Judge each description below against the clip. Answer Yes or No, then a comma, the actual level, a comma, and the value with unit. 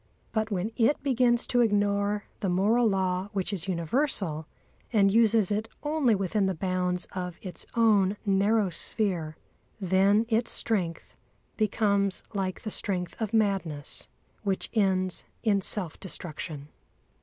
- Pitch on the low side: No, high, 200 Hz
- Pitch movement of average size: Yes, average, 3.0 semitones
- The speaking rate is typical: No, slow, 130 wpm